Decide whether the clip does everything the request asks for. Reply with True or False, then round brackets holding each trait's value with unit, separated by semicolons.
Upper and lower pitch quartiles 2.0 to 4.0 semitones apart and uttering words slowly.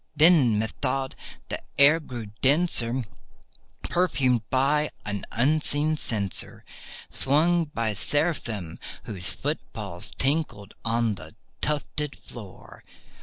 False (5.4 semitones; 100 wpm)